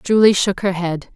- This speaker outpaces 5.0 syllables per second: No, 4.5 syllables/s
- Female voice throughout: Yes, female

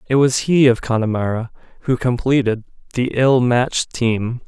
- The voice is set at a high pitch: No, low, 125 Hz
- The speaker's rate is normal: Yes, average, 150 wpm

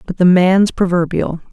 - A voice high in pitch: No, medium, 180 Hz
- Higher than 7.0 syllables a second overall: No, 4.6 syllables/s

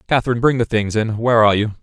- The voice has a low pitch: Yes, low, 115 Hz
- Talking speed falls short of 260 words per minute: No, fast, 265 wpm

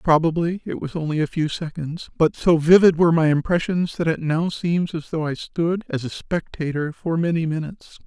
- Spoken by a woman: No, male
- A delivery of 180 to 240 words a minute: Yes, average, 200 wpm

